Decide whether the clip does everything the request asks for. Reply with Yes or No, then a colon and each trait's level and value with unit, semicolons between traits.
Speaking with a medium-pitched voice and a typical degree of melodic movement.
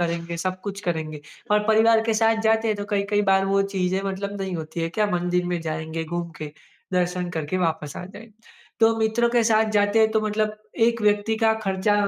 No: high, 195 Hz; average, 3.9 semitones